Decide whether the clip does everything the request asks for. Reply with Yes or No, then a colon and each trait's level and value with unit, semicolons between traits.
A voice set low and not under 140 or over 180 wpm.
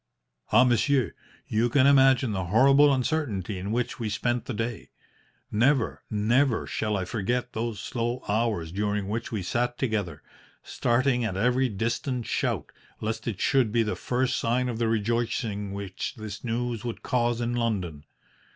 Yes: low, 115 Hz; average, 160 wpm